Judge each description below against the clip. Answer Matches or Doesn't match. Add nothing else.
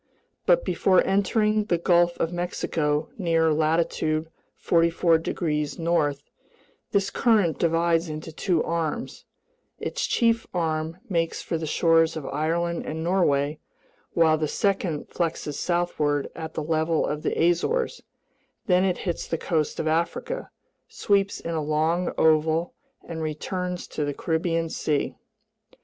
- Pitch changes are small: Matches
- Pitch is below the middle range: Doesn't match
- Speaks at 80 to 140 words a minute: Matches